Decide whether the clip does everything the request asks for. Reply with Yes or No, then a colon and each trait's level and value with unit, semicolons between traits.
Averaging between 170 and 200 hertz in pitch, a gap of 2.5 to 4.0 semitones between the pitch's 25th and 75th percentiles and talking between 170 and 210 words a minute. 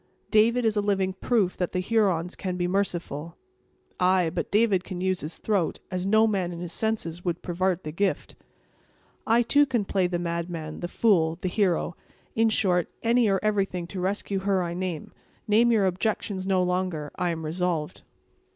Yes: medium, 185 Hz; average, 2.9 semitones; average, 180 wpm